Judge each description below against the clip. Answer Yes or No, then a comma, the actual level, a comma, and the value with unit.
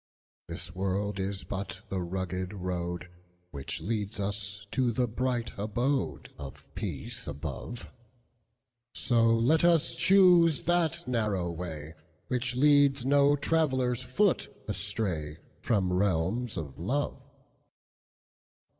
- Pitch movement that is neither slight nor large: No, wide, 5.8 semitones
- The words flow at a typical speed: No, slow, 95 wpm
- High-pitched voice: No, low, 105 Hz